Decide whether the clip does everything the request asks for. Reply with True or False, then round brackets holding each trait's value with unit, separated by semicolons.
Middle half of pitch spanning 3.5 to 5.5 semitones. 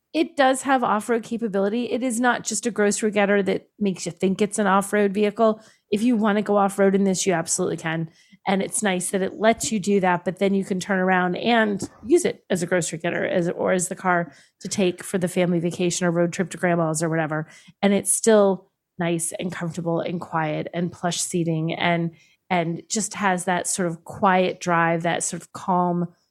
False (2.9 semitones)